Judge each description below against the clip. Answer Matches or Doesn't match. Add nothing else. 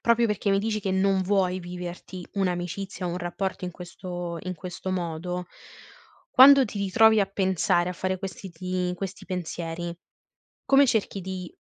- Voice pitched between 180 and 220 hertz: Matches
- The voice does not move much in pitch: Matches